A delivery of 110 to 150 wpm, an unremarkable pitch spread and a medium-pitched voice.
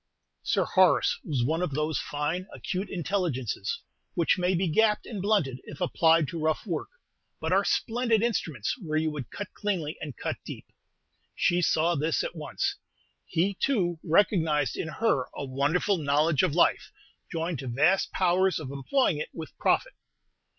No: average, 165 wpm; average, 4.2 semitones; medium, 165 Hz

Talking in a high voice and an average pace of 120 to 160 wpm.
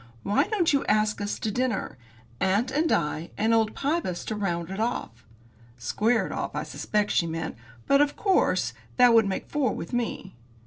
No: high, 215 Hz; average, 185 wpm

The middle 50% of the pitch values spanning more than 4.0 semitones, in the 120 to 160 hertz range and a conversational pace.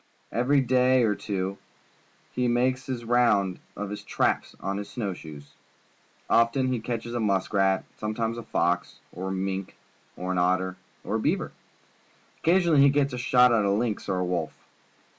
No: average, 4.5 semitones; low, 110 Hz; average, 180 wpm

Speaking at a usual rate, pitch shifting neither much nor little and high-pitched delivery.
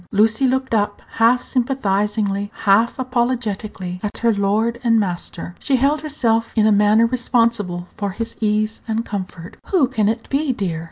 Yes: average, 160 wpm; average, 3.1 semitones; high, 225 Hz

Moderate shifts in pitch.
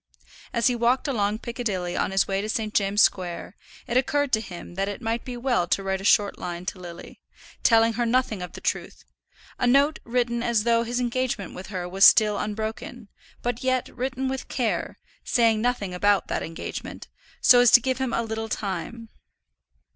Yes: average, 3.8 semitones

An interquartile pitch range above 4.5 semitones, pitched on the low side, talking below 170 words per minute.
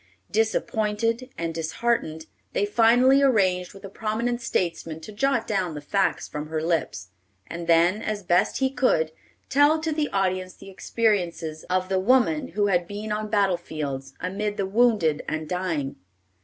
No: average, 5.1 semitones; high, 195 Hz; average, 160 wpm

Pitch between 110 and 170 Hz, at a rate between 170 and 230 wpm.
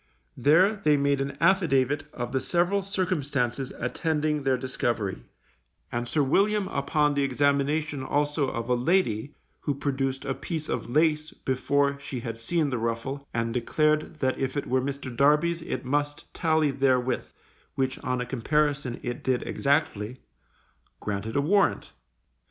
No: medium, 140 Hz; average, 150 wpm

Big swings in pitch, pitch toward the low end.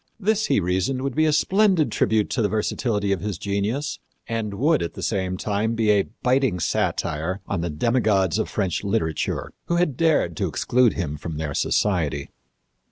Yes: wide, 6.0 semitones; low, 105 Hz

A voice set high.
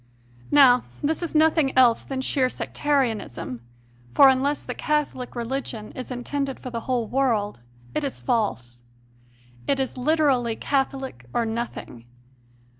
Yes: very high, 260 Hz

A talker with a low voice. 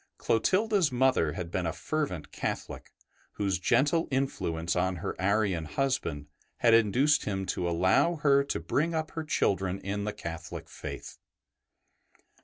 Yes: low, 105 Hz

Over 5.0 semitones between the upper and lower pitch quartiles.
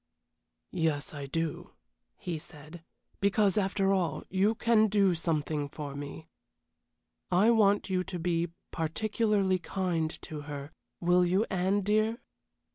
No: average, 4.0 semitones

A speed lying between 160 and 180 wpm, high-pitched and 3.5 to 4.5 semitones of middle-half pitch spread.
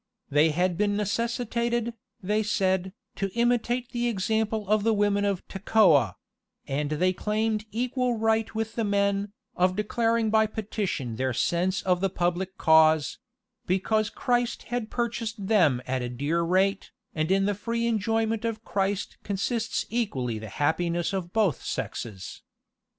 No: average, 150 wpm; high, 205 Hz; average, 4.1 semitones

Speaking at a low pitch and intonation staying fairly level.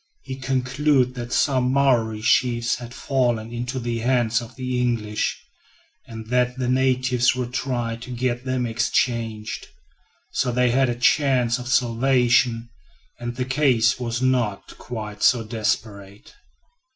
Yes: low, 120 Hz; narrow, 1.7 semitones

